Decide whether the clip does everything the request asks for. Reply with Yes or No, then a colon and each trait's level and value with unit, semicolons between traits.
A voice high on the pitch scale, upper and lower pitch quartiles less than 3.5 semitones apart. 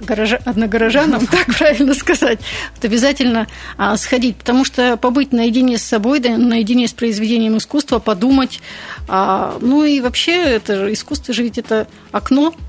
Yes: high, 245 Hz; average, 3.1 semitones